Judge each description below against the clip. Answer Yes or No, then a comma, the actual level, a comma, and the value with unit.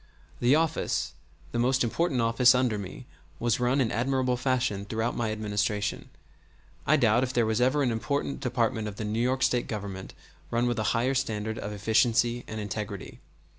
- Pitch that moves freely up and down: No, average, 2.8 semitones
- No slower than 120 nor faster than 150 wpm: No, average, 175 wpm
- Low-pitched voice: Yes, low, 120 Hz